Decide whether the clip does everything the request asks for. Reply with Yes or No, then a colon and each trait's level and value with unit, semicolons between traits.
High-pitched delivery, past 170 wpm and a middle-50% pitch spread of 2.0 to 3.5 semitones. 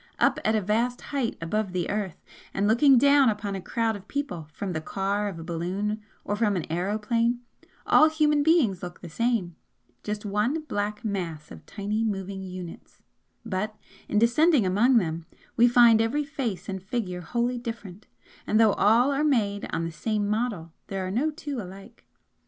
No: high, 210 Hz; average, 180 wpm; average, 4.0 semitones